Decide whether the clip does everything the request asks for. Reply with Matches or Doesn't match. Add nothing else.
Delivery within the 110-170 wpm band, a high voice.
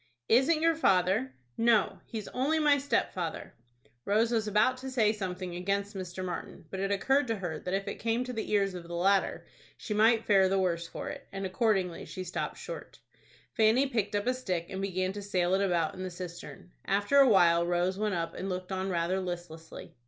Doesn't match